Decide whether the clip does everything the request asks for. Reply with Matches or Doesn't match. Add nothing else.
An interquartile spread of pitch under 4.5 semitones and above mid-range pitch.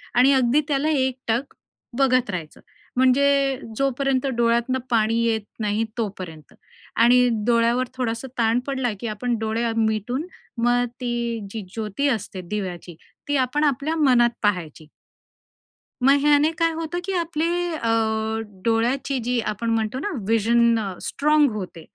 Matches